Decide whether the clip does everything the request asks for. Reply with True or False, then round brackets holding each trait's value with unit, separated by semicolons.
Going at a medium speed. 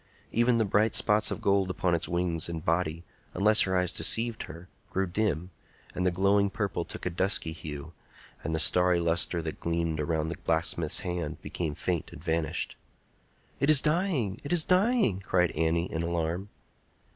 True (175 wpm)